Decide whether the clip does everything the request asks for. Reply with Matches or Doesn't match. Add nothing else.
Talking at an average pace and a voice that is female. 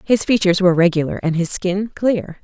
Matches